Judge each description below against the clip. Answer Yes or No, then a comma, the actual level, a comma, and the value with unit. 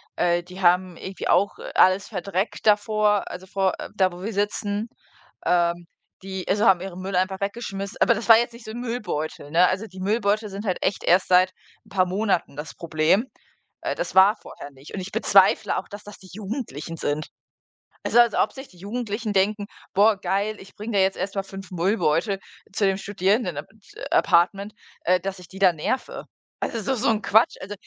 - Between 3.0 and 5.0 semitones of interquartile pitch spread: No, narrow, 2.5 semitones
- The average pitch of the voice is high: Yes, high, 195 Hz